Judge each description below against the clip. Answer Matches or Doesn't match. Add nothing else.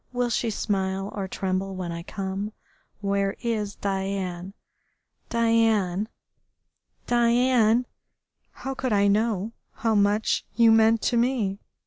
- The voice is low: Doesn't match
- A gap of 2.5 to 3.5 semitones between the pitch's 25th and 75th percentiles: Matches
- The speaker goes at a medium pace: Doesn't match